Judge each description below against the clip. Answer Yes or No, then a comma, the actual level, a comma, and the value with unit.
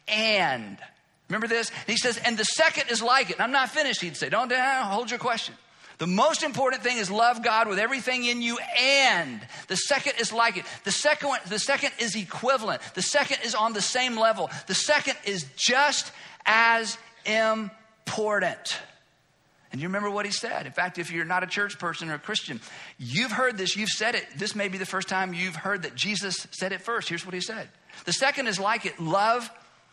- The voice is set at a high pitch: Yes, high, 220 Hz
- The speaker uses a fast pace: Yes, fast, 210 wpm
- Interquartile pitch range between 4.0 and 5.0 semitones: Yes, average, 4.4 semitones